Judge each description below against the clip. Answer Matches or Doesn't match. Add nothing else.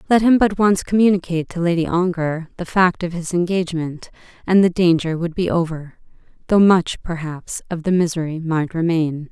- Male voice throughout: Doesn't match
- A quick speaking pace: Doesn't match